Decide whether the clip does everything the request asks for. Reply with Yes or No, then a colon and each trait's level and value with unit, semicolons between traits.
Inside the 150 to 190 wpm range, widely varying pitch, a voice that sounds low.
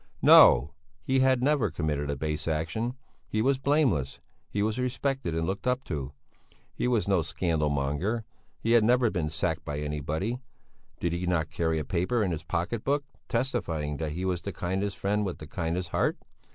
Yes: average, 185 wpm; wide, 7.0 semitones; very low, 90 Hz